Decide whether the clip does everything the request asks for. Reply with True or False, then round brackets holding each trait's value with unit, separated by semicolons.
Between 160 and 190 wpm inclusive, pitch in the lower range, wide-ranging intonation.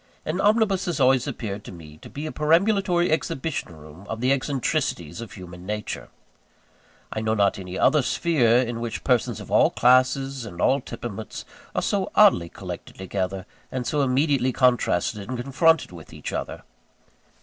True (165 wpm; 125 Hz; 6.4 semitones)